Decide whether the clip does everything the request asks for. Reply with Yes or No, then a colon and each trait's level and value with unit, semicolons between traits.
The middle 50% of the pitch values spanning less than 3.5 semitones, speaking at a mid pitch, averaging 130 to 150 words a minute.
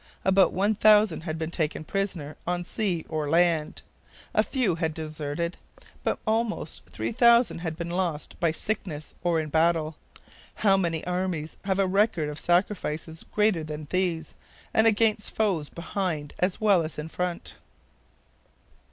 No: average, 3.8 semitones; medium, 175 Hz; average, 145 wpm